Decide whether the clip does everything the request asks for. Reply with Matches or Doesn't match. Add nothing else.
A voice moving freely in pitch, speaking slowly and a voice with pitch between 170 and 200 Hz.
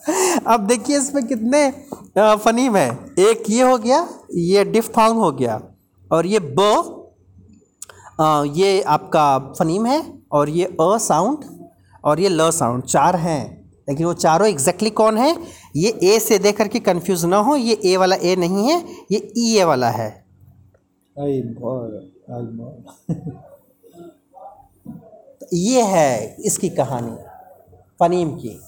Doesn't match